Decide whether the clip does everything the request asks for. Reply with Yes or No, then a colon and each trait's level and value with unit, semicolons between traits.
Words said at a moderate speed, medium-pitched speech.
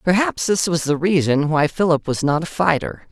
No: fast, 210 wpm; medium, 165 Hz